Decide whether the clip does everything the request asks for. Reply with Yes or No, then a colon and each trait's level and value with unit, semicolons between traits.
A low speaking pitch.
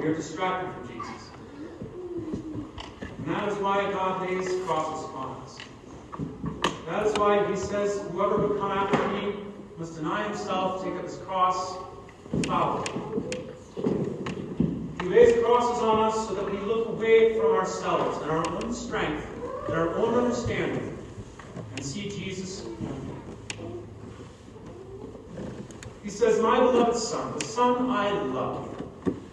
No: high, 200 Hz